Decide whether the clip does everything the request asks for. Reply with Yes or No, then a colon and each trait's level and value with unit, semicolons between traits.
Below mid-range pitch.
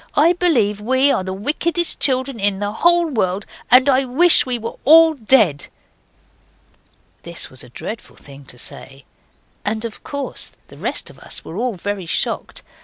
No: high, 230 Hz